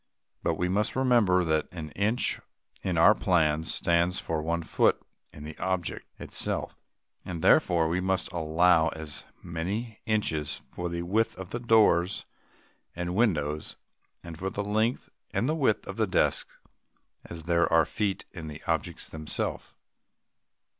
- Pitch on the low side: Yes, very low, 90 Hz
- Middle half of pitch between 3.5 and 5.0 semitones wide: Yes, average, 3.9 semitones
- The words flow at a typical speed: Yes, average, 145 wpm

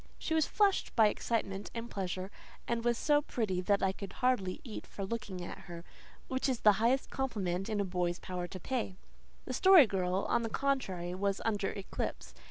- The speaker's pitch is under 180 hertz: No, high, 205 Hz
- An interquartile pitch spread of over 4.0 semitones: Yes, average, 4.4 semitones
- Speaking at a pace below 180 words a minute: No, average, 190 wpm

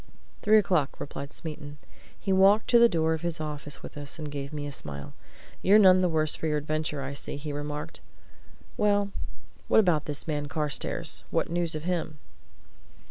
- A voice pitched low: No, medium, 155 Hz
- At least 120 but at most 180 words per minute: No, average, 190 wpm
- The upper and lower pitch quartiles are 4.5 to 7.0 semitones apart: No, average, 3.6 semitones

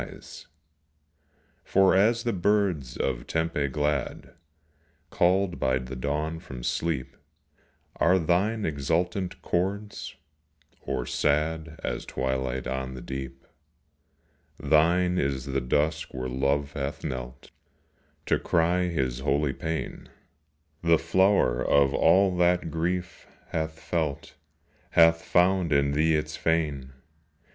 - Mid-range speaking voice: No, very low, 80 Hz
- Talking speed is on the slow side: Yes, slow, 115 wpm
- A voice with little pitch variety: No, average, 4.6 semitones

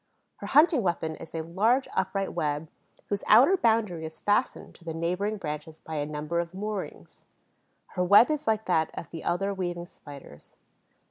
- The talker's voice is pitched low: No, medium, 180 Hz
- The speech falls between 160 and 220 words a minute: Yes, average, 175 wpm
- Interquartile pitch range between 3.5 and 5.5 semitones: Yes, average, 4.7 semitones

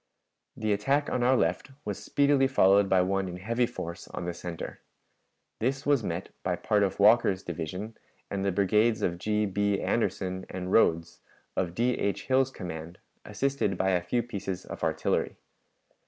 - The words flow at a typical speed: Yes, average, 170 wpm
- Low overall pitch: Yes, low, 100 Hz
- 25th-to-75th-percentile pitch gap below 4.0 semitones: No, average, 4.6 semitones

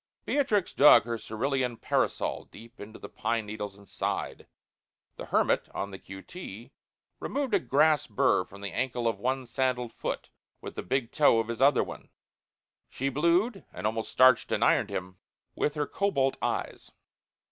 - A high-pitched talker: No, low, 125 Hz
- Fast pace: No, average, 170 wpm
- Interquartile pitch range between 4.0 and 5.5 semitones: Yes, average, 5.1 semitones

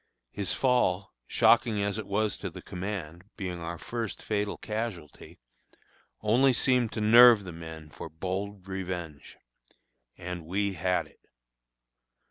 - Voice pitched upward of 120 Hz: No, low, 100 Hz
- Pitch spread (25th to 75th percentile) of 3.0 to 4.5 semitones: Yes, average, 3.7 semitones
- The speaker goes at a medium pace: No, slow, 130 wpm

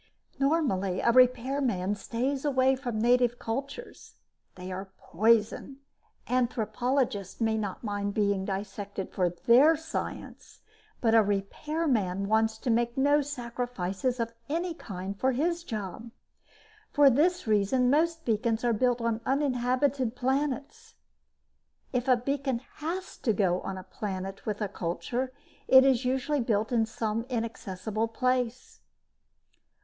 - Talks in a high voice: Yes, high, 235 Hz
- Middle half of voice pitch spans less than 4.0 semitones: No, average, 4.3 semitones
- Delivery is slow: Yes, slow, 130 wpm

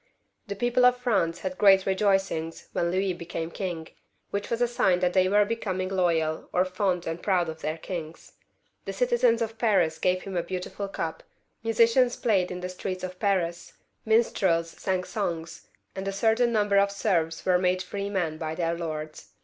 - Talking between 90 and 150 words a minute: No, average, 180 wpm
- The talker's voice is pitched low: No, medium, 185 Hz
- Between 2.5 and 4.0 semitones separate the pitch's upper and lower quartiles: Yes, average, 3.2 semitones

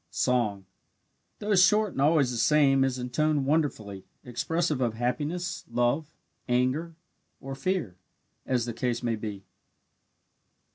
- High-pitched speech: No, low, 135 Hz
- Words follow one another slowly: Yes, slow, 130 wpm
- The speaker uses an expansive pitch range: No, average, 4.4 semitones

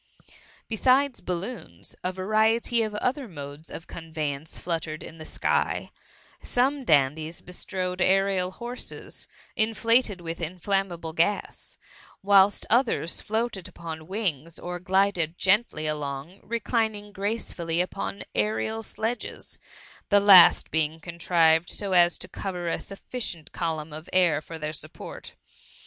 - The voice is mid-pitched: Yes, medium, 180 Hz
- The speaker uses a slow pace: Yes, slow, 120 wpm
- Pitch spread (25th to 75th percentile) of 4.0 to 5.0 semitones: Yes, average, 4.5 semitones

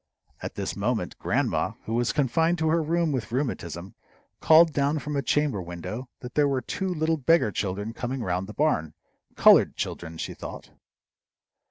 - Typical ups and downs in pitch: No, wide, 7.2 semitones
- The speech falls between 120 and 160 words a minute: No, average, 170 wpm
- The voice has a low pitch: Yes, low, 130 Hz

